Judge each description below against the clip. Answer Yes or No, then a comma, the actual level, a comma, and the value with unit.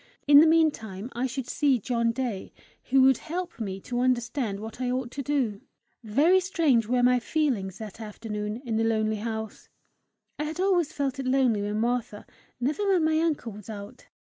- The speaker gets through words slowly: No, average, 185 wpm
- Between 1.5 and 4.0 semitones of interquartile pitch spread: No, average, 4.7 semitones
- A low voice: No, high, 245 Hz